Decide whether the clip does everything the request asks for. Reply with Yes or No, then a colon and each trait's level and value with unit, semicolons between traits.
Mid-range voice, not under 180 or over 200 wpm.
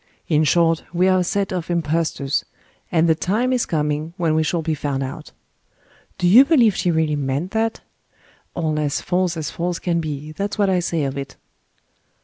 Yes: medium, 165 Hz; average, 190 wpm